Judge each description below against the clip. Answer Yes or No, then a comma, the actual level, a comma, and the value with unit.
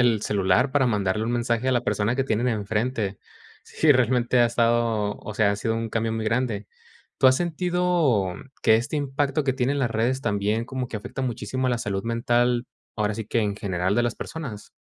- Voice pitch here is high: No, low, 115 Hz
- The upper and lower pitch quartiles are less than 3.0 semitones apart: No, average, 3.4 semitones